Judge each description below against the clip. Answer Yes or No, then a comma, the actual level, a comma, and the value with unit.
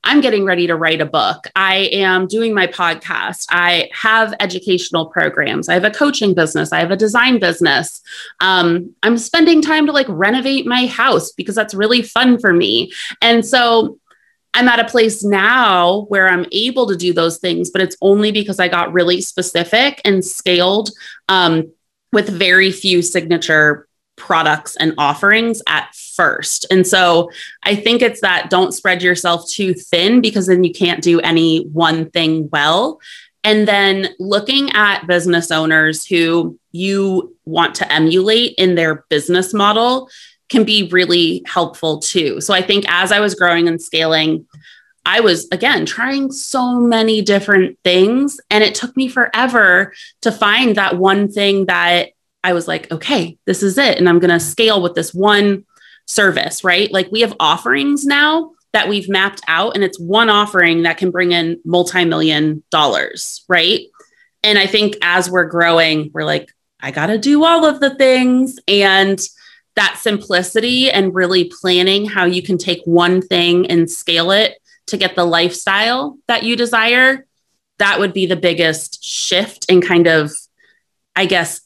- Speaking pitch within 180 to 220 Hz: Yes, high, 190 Hz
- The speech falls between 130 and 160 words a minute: No, average, 170 wpm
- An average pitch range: Yes, average, 4.5 semitones